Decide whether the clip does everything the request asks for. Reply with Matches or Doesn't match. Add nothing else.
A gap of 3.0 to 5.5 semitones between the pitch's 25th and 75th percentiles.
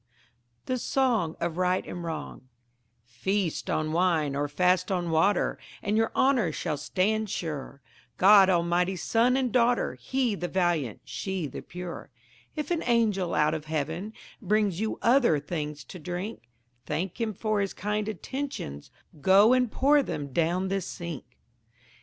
Matches